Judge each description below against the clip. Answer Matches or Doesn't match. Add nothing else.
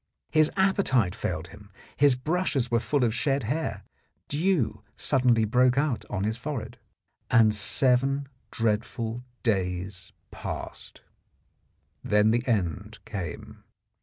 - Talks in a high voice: Doesn't match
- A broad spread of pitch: Doesn't match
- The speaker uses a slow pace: Matches